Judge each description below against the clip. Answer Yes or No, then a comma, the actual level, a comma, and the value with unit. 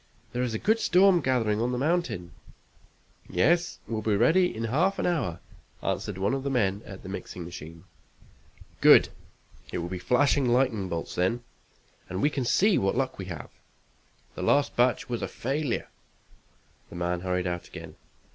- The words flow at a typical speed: Yes, average, 175 wpm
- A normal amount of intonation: No, wide, 7.1 semitones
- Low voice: Yes, low, 115 Hz